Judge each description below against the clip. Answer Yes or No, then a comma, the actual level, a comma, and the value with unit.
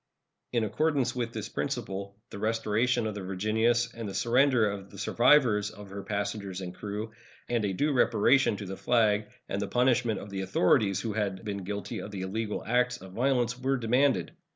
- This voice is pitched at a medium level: No, low, 110 Hz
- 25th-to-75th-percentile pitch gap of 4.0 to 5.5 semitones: No, average, 3.5 semitones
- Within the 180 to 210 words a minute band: Yes, average, 190 wpm